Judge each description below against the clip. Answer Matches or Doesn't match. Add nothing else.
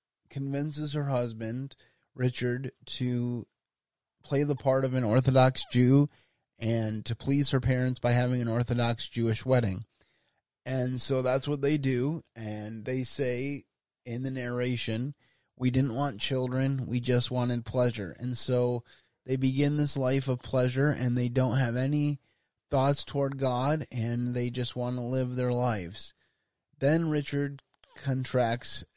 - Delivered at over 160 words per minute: Doesn't match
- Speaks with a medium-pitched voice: Doesn't match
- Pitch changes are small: Matches